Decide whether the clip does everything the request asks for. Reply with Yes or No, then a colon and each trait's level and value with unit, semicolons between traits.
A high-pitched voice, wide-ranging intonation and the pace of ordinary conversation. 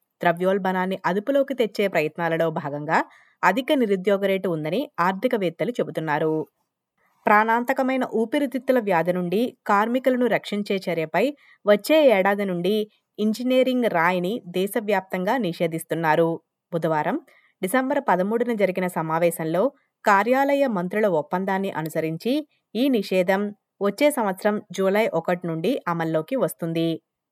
Yes: high, 195 Hz; wide, 6.1 semitones; average, 95 wpm